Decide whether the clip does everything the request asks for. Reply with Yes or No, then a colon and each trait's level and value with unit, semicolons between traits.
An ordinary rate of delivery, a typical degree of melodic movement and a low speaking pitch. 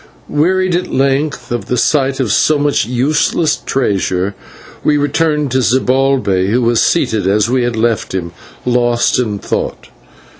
Yes: average, 150 wpm; average, 4.5 semitones; low, 125 Hz